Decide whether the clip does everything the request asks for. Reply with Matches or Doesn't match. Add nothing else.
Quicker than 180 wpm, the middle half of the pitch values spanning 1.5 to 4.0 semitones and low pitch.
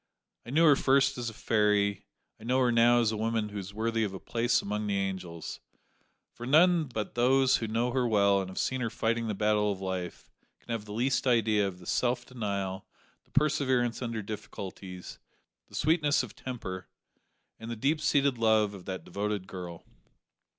Matches